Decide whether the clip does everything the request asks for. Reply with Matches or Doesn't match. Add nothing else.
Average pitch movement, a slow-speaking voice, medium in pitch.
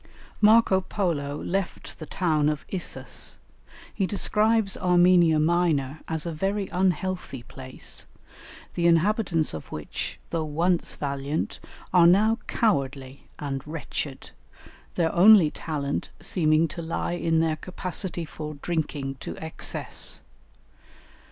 Matches